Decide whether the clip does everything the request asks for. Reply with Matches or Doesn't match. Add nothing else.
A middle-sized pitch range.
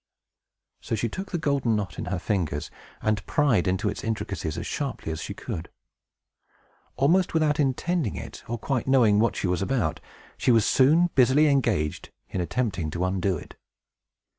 Doesn't match